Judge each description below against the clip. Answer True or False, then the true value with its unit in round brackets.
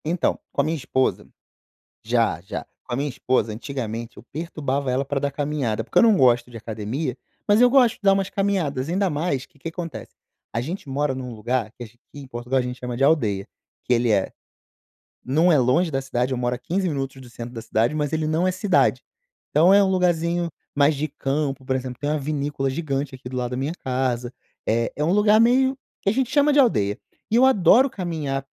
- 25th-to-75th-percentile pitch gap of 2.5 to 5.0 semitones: False (5.5 semitones)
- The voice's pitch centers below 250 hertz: True (140 Hz)